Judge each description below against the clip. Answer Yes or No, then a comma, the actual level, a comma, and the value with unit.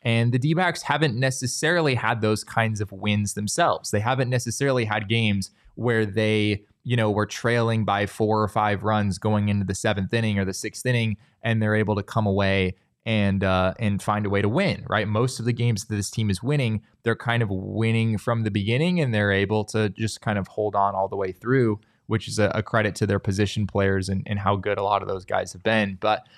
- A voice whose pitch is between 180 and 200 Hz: No, low, 110 Hz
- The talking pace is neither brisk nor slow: No, fast, 230 wpm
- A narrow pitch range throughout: Yes, narrow, 2.3 semitones